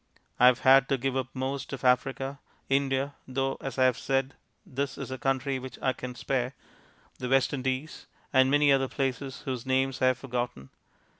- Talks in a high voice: No, low, 130 Hz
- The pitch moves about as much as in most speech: No, narrow, 0.9 semitones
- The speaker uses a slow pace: No, average, 190 wpm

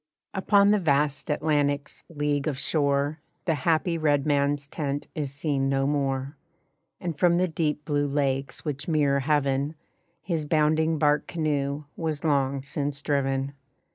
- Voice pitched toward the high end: No, medium, 145 Hz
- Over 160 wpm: No, average, 140 wpm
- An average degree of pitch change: No, narrow, 2.0 semitones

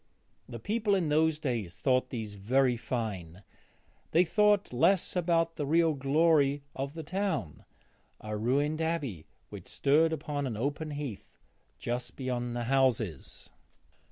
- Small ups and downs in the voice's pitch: No, average, 5.1 semitones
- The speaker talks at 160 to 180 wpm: No, slow, 135 wpm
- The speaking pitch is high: No, medium, 140 Hz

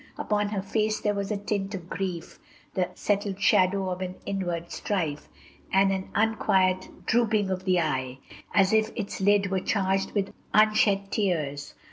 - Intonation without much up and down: Yes, narrow, 1.9 semitones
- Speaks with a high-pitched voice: Yes, high, 195 Hz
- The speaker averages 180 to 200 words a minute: No, average, 160 wpm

